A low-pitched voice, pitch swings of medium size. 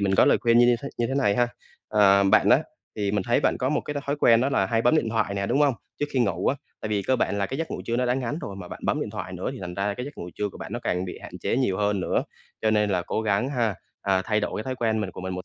Yes: low, 110 Hz; average, 4.0 semitones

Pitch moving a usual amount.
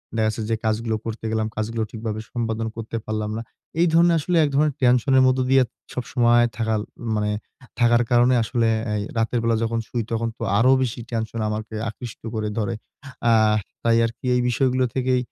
No: narrow, 2.1 semitones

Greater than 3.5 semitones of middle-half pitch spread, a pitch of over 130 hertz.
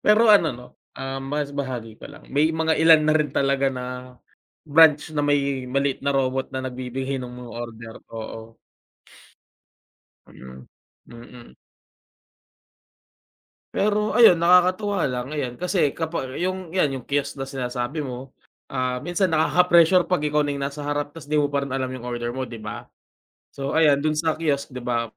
Yes: average, 4.1 semitones; medium, 140 Hz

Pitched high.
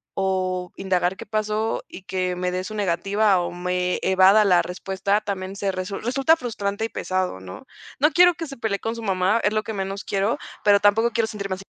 Yes: high, 195 Hz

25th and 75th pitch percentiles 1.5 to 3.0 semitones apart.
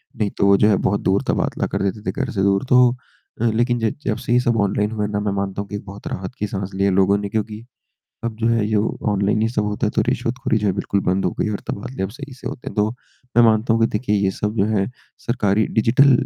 Yes: narrow, 2.4 semitones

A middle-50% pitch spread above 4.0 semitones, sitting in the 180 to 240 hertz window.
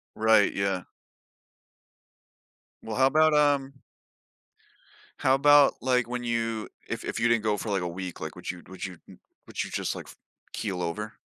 No: wide, 5.5 semitones; low, 110 Hz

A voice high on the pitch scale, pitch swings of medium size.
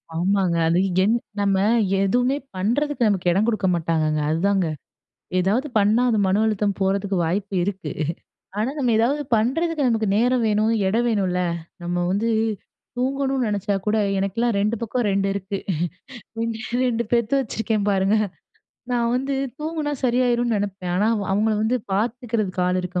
Yes: high, 215 Hz; average, 3.8 semitones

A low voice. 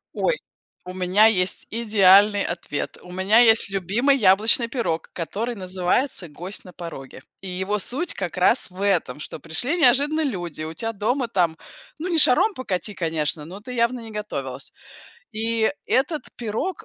No: high, 205 Hz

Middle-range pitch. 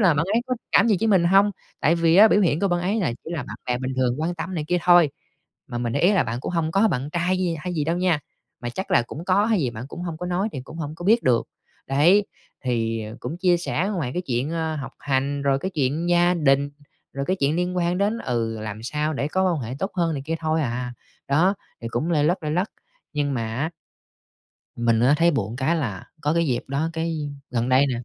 Yes: medium, 155 Hz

